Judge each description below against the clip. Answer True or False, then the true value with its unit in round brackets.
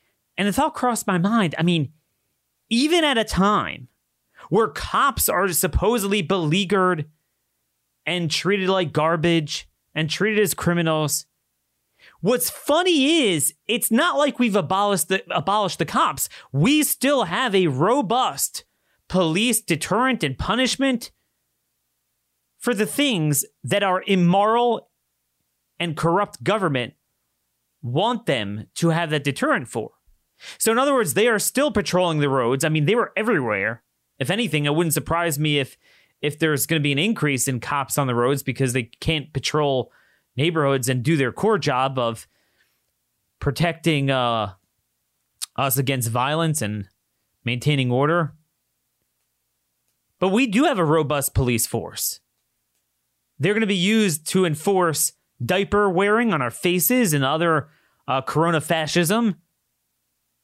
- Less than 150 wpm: True (140 wpm)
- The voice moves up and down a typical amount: False (7.3 semitones)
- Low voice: False (160 Hz)